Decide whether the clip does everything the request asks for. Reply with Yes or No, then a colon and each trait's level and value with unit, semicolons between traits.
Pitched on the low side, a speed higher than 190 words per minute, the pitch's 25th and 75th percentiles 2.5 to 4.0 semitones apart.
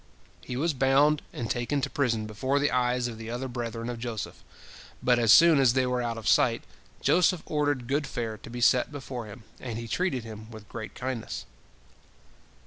Yes: low, 125 Hz; average, 200 wpm; average, 2.9 semitones